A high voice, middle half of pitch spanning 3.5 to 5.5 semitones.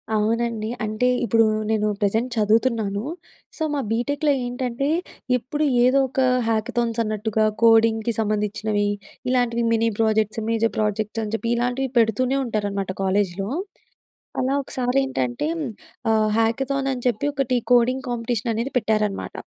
No: high, 225 Hz; average, 2.7 semitones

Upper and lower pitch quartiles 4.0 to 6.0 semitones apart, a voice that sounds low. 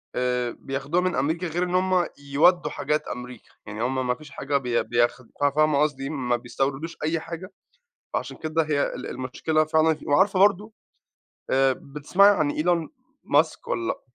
No: average, 4.4 semitones; medium, 150 Hz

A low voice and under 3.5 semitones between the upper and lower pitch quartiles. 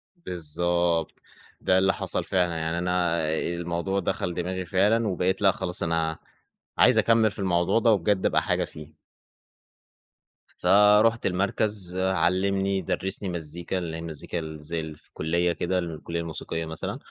Yes: very low, 90 Hz; narrow, 2.6 semitones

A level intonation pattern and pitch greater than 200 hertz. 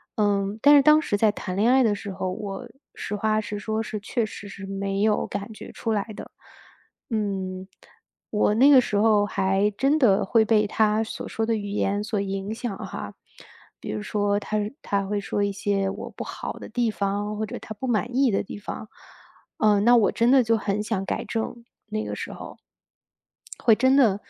Yes: narrow, 2.1 semitones; high, 210 Hz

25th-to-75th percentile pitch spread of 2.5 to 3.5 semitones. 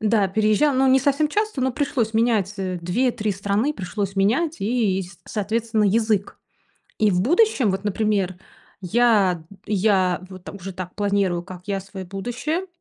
No: average, 4.0 semitones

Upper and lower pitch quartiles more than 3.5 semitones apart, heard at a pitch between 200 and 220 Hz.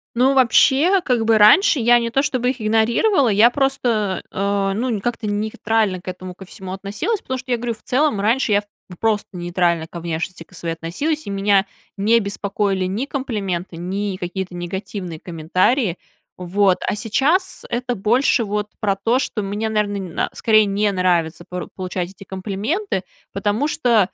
Yes: average, 4.3 semitones; high, 205 Hz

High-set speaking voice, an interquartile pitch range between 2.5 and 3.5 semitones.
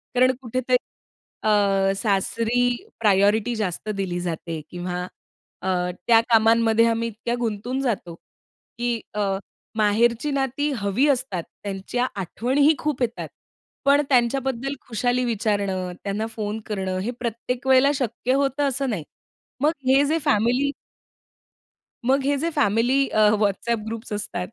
No: high, 230 Hz; average, 4.1 semitones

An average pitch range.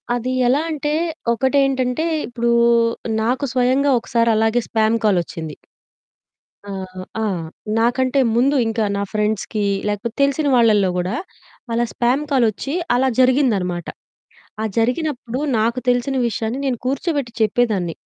Yes: average, 3.4 semitones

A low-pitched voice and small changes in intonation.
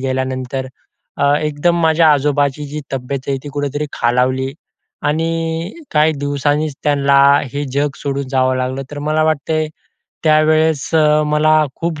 No: medium, 145 Hz; narrow, 2.3 semitones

